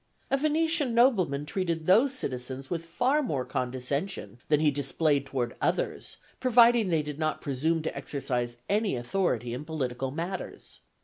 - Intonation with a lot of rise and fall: Yes, wide, 8.2 semitones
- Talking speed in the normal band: Yes, average, 145 wpm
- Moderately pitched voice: Yes, medium, 155 Hz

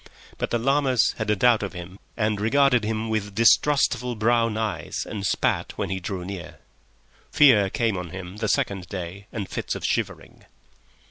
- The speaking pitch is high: No, low, 105 Hz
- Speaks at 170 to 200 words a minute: Yes, average, 175 wpm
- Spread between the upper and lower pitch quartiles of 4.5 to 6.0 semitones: No, average, 3.3 semitones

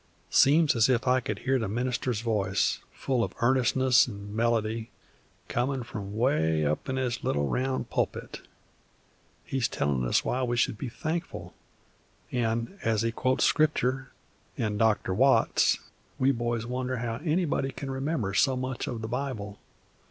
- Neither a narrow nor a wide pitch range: Yes, average, 3.1 semitones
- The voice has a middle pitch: No, low, 120 Hz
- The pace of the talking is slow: No, average, 155 wpm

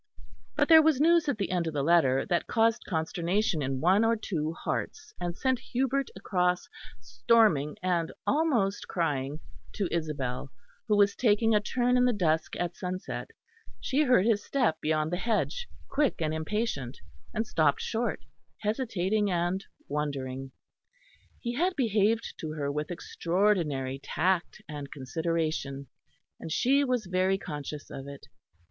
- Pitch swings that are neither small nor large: No, wide, 6.8 semitones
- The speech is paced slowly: No, average, 150 wpm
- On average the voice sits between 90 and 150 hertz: No, medium, 180 Hz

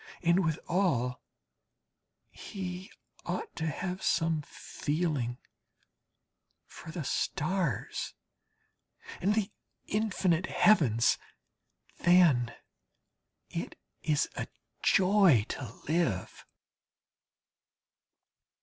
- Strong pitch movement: No, average, 4.9 semitones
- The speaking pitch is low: No, medium, 170 Hz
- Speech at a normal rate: No, slow, 70 wpm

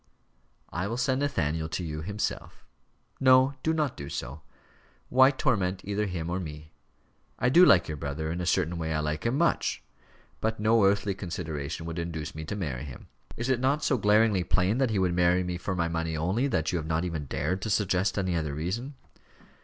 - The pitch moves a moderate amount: No, wide, 5.7 semitones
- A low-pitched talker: Yes, very low, 90 Hz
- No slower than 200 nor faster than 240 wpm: Yes, fast, 205 wpm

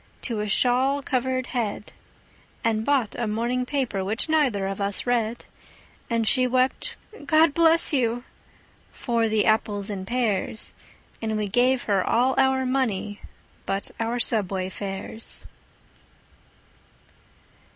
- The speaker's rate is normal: No, slow, 125 wpm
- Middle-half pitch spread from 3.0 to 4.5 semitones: Yes, average, 3.6 semitones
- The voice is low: No, high, 230 Hz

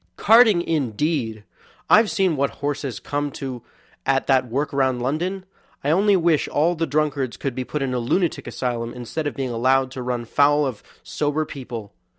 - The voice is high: No, medium, 140 Hz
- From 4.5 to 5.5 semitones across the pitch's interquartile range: No, average, 3.7 semitones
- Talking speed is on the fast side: No, average, 175 wpm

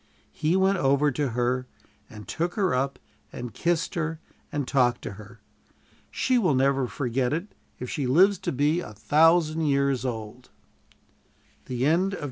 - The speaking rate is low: No, average, 155 wpm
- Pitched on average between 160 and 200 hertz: No, medium, 140 Hz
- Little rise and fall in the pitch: No, average, 4.8 semitones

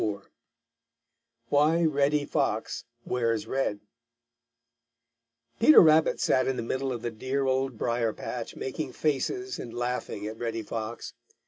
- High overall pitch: No, low, 130 Hz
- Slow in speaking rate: Yes, slow, 130 wpm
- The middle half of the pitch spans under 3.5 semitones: No, average, 3.9 semitones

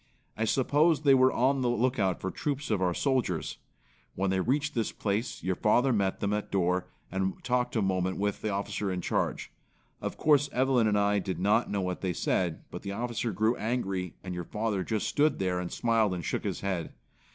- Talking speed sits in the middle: No, fast, 210 wpm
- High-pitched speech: No, low, 105 Hz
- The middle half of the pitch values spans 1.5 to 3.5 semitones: No, average, 4.7 semitones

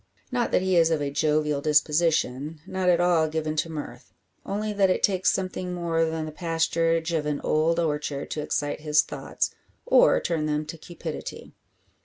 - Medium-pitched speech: Yes, medium, 160 Hz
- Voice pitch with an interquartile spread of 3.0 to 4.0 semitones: No, narrow, 2.4 semitones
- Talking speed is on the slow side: No, average, 180 wpm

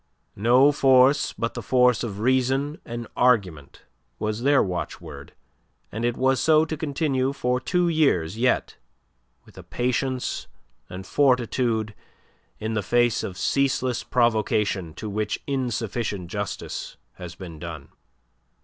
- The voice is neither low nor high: No, low, 120 Hz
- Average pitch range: Yes, average, 4.3 semitones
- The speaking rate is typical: No, slow, 130 wpm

